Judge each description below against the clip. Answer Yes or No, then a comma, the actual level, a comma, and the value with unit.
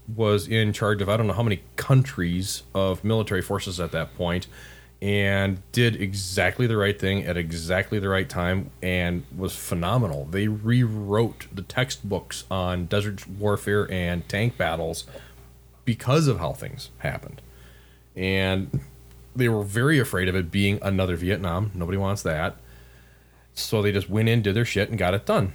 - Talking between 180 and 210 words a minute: No, average, 165 wpm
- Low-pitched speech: Yes, very low, 95 Hz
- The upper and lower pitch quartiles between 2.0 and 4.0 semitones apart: Yes, average, 3.3 semitones